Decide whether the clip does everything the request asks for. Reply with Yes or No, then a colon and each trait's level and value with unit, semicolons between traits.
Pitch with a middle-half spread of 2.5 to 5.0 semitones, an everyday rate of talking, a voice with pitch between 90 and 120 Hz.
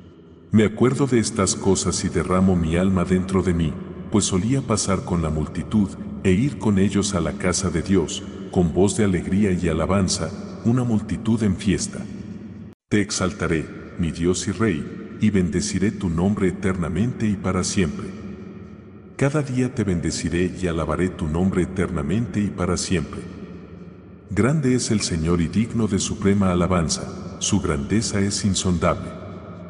Yes: average, 2.8 semitones; average, 155 wpm; very low, 95 Hz